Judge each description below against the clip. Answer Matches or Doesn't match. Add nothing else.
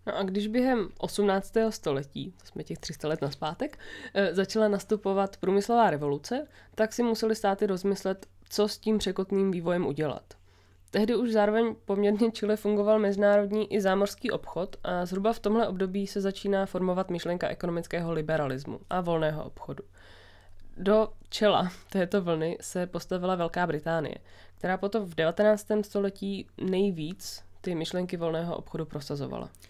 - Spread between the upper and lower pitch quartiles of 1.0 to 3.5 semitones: Doesn't match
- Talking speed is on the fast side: Doesn't match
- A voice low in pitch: Doesn't match